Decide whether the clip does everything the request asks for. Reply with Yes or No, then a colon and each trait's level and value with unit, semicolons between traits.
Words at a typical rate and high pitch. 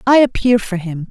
No: fast, 220 wpm; high, 215 Hz